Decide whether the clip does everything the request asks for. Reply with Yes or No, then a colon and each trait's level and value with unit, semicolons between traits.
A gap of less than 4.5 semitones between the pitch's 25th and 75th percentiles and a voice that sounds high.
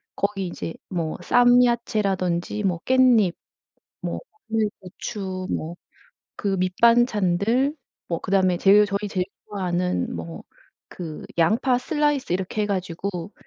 Yes: average, 4.0 semitones; high, 195 Hz